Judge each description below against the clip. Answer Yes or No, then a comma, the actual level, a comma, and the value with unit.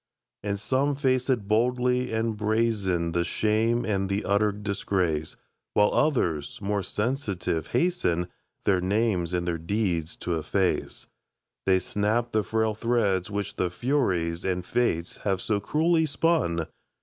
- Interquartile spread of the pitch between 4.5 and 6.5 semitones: Yes, average, 4.8 semitones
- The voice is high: No, low, 105 Hz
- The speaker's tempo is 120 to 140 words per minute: Yes, slow, 135 wpm